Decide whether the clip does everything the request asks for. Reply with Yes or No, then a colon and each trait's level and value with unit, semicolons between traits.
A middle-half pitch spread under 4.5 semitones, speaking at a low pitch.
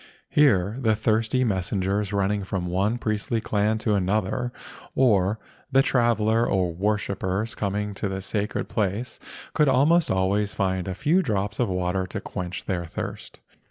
Yes: average, 3.1 semitones; low, 105 Hz